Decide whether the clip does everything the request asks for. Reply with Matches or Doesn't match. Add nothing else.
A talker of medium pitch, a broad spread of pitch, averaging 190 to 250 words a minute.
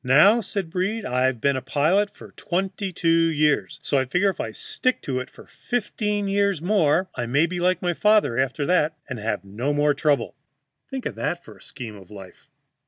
Matches